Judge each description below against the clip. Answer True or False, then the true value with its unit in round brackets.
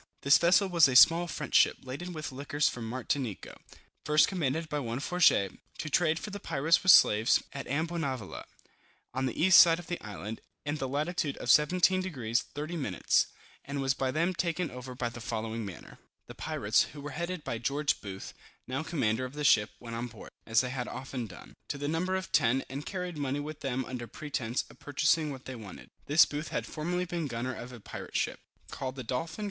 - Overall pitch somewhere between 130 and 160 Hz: True (140 Hz)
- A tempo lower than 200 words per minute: False (205 wpm)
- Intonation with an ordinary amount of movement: True (4.8 semitones)